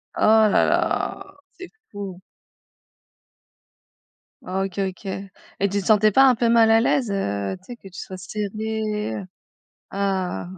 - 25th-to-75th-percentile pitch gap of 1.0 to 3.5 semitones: Yes, average, 2.7 semitones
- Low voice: No, high, 200 Hz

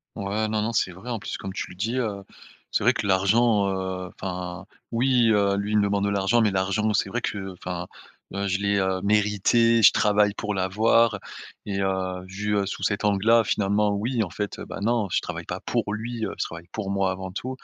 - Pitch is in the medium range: No, low, 100 Hz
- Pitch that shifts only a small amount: Yes, narrow, 2.2 semitones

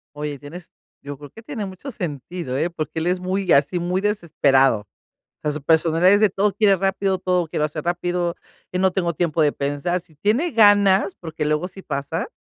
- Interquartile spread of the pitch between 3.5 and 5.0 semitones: Yes, average, 4.1 semitones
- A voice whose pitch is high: No, medium, 175 Hz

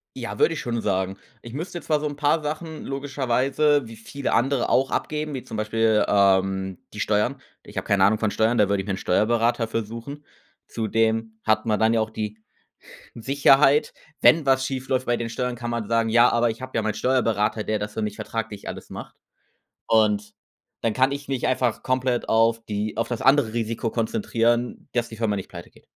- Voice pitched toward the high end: No, low, 115 Hz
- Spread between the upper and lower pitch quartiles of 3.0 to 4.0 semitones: Yes, average, 3.3 semitones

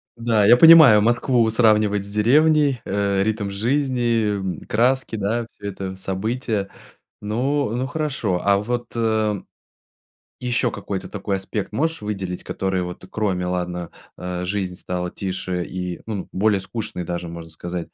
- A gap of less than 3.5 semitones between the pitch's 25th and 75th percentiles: No, average, 4.2 semitones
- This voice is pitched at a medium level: No, low, 105 Hz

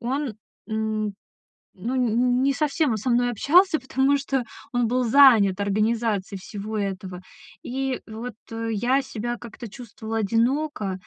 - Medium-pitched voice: No, high, 235 Hz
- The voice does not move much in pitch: No, average, 3.6 semitones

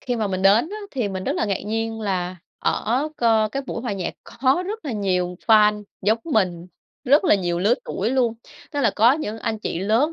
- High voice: Yes, high, 220 Hz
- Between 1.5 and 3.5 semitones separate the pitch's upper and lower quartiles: No, average, 4.2 semitones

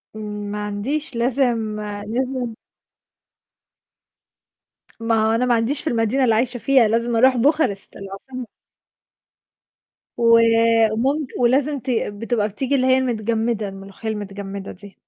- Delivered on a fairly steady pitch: No, average, 3.5 semitones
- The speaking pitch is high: Yes, high, 230 Hz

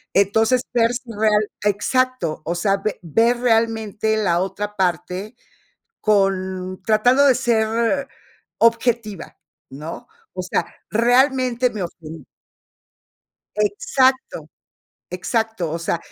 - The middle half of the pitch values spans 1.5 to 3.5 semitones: No, average, 4.1 semitones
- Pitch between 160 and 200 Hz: No, high, 215 Hz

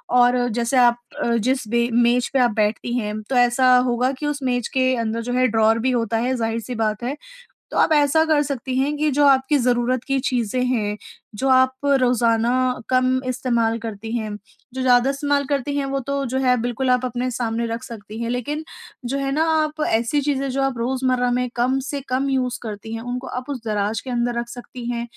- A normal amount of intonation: No, narrow, 2.2 semitones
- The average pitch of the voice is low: No, very high, 250 Hz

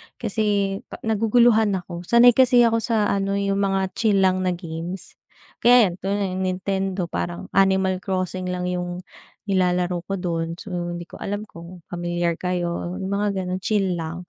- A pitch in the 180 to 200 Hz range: Yes, high, 190 Hz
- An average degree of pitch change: No, narrow, 2.3 semitones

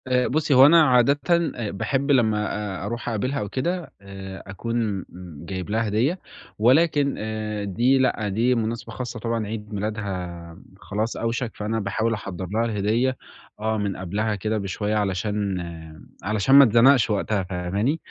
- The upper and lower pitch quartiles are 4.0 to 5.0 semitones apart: No, average, 3.5 semitones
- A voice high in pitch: No, low, 110 Hz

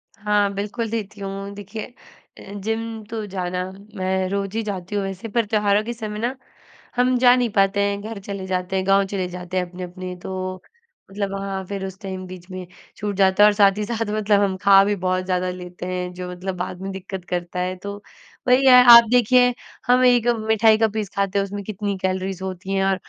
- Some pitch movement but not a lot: No, narrow, 2.3 semitones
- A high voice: Yes, high, 195 Hz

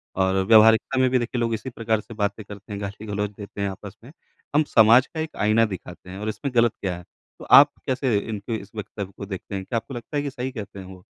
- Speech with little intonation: No, average, 3.2 semitones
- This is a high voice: No, low, 110 Hz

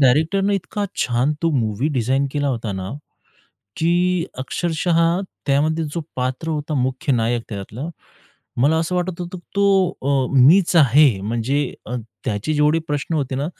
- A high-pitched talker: No, medium, 145 Hz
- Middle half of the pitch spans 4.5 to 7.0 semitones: Yes, average, 4.8 semitones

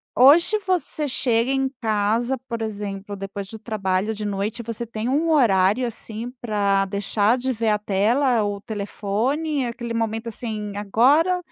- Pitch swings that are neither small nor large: Yes, average, 3.6 semitones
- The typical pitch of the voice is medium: No, high, 225 Hz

